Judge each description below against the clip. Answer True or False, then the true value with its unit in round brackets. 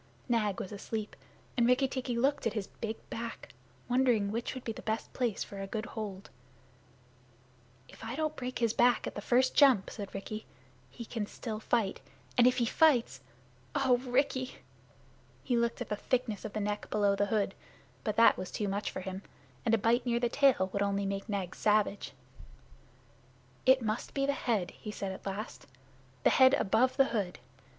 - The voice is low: False (225 Hz)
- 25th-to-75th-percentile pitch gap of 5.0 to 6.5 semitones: False (3.5 semitones)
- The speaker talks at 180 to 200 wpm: True (190 wpm)